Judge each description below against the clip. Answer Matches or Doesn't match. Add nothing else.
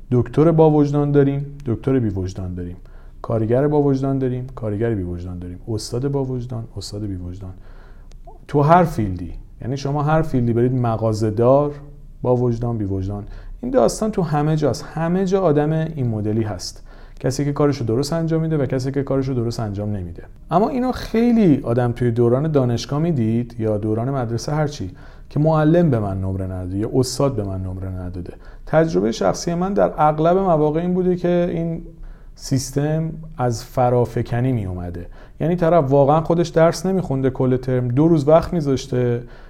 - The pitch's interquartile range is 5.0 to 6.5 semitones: Matches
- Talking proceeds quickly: Matches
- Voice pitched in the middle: Doesn't match